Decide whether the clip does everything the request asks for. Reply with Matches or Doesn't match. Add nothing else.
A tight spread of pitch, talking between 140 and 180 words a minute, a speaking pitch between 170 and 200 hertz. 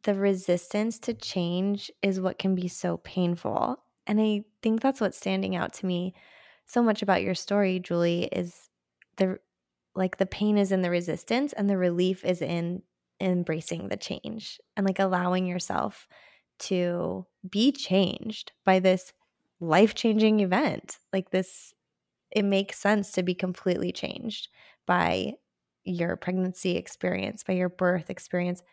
Matches